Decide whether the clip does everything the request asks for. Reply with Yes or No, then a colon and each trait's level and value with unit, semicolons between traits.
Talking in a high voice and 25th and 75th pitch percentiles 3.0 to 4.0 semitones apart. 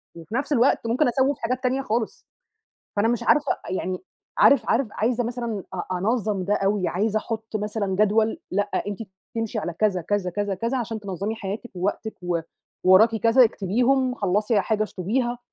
Yes: high, 220 Hz; average, 3.5 semitones